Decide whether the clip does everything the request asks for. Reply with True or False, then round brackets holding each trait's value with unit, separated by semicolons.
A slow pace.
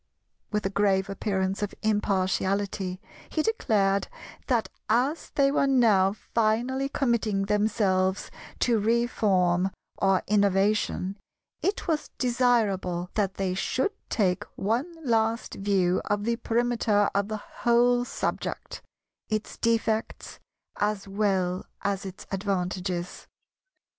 True (110 wpm)